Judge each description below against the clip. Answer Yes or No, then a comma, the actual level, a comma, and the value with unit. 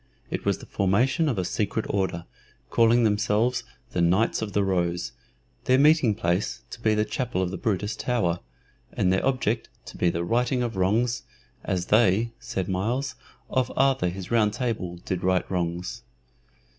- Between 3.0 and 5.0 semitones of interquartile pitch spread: Yes, average, 4.6 semitones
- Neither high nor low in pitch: No, low, 105 Hz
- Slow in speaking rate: No, average, 170 wpm